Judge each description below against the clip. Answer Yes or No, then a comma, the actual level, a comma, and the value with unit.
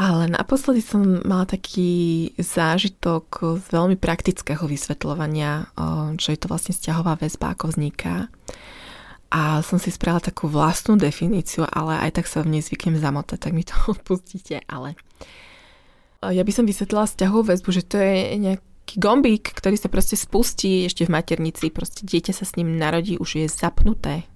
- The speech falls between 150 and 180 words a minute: Yes, average, 160 wpm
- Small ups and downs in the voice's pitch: No, average, 3.2 semitones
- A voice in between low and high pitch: Yes, medium, 170 Hz